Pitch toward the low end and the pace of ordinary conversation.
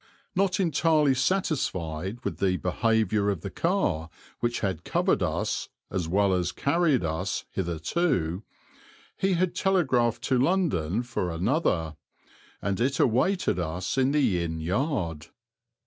No: low, 110 Hz; slow, 130 wpm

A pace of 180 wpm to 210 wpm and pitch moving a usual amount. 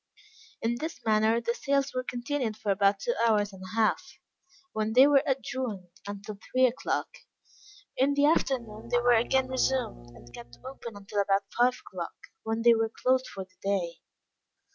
No: average, 170 wpm; average, 4.1 semitones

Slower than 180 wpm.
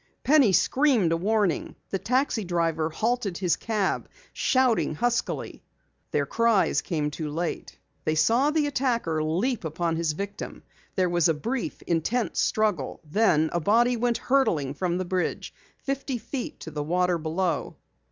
Yes: average, 150 wpm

